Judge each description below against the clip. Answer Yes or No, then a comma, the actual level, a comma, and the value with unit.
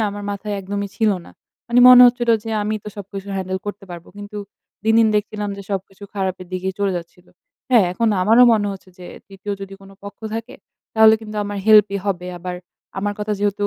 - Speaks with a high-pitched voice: Yes, high, 205 Hz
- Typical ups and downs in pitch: No, narrow, 1.9 semitones